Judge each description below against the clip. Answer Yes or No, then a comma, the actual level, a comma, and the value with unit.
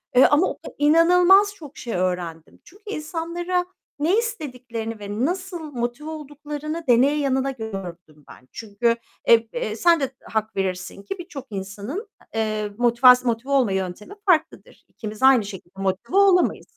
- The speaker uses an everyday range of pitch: No, wide, 7.4 semitones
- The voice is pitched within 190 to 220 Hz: No, very high, 255 Hz